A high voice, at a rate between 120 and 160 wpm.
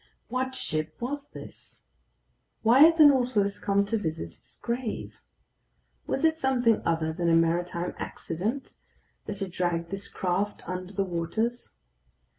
Yes: high, 200 Hz; average, 140 wpm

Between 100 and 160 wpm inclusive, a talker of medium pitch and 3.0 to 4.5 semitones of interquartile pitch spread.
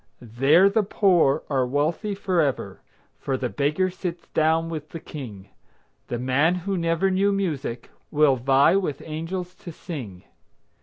No: average, 145 wpm; medium, 160 Hz; average, 5.0 semitones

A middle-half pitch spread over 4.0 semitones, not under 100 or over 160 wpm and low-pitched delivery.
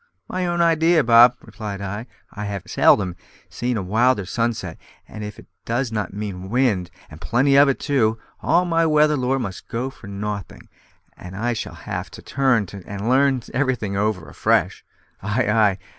No: average, 4.8 semitones; average, 175 wpm; low, 115 Hz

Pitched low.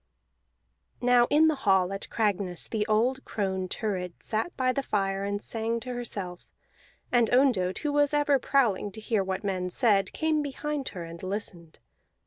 No: high, 215 Hz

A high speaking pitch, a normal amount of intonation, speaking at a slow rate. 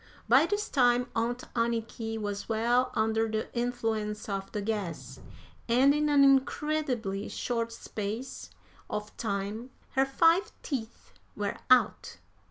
Yes: high, 230 Hz; average, 3.4 semitones; slow, 125 wpm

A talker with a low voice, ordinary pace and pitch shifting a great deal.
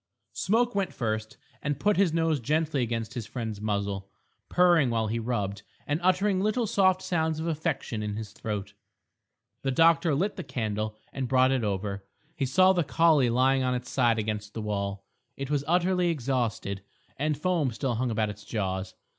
Yes: low, 130 Hz; average, 180 wpm; wide, 7.2 semitones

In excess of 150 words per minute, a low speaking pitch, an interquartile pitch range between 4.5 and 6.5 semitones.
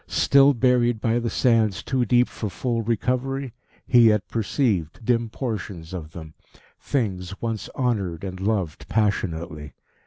No: slow, 135 wpm; low, 110 Hz; average, 4.8 semitones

